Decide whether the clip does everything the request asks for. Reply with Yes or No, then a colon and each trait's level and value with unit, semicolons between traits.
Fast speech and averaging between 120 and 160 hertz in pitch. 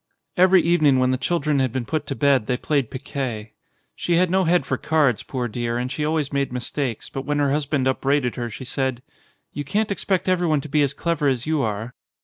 Yes: fast, 220 wpm; medium, 140 Hz